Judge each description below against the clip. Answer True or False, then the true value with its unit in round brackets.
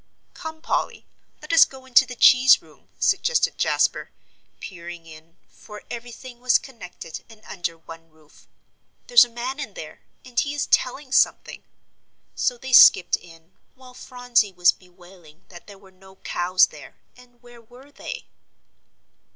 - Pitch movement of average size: False (6.5 semitones)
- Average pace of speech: True (150 wpm)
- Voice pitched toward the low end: False (235 Hz)